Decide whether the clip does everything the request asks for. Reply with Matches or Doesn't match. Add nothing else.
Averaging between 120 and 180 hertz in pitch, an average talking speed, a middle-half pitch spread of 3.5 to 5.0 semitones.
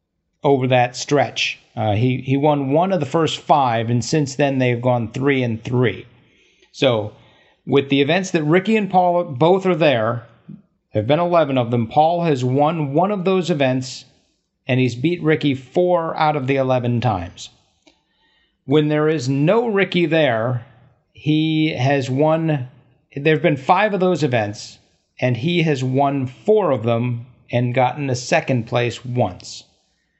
Matches